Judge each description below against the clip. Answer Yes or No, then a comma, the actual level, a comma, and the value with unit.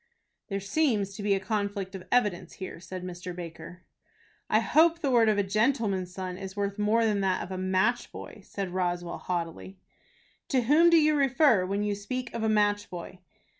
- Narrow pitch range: No, average, 3.7 semitones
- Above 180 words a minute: Yes, average, 195 wpm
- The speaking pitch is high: Yes, high, 200 Hz